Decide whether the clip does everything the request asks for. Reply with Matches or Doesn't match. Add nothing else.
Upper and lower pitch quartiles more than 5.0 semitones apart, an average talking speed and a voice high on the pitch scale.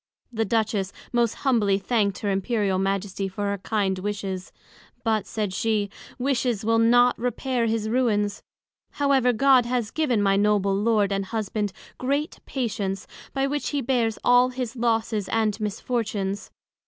Doesn't match